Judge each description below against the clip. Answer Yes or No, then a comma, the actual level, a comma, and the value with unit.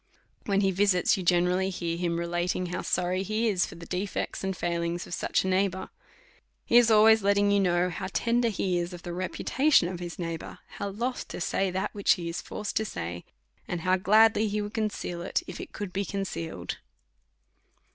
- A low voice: No, medium, 185 Hz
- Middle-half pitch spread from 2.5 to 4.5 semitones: Yes, average, 2.8 semitones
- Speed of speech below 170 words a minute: No, fast, 205 wpm